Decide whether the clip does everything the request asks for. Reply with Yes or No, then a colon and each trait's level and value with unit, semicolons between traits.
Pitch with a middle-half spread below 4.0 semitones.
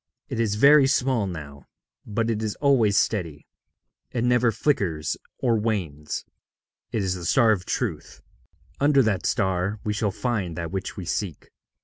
No: average, 4.7 semitones